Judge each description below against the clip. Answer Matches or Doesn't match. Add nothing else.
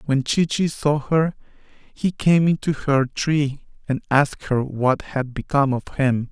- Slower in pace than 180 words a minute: Matches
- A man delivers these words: Matches